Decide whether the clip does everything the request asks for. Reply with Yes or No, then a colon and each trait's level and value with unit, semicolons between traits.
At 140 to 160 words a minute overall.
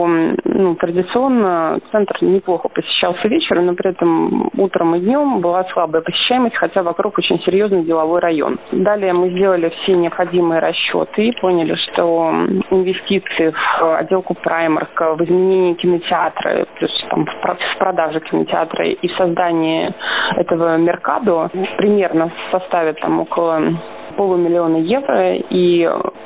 No: average, 130 wpm